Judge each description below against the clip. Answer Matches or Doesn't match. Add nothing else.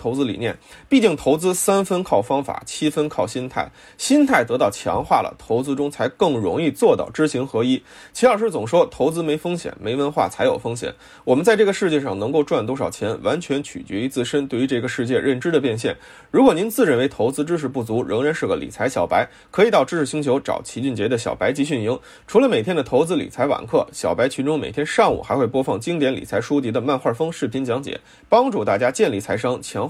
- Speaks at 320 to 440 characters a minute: Matches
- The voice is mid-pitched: Matches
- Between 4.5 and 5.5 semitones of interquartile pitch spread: Matches